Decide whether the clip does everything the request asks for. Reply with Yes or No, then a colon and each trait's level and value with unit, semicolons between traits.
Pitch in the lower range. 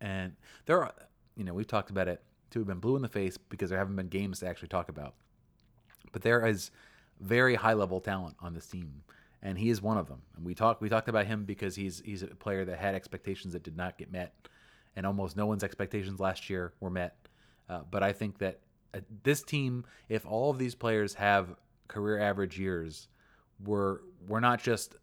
Yes: low, 100 Hz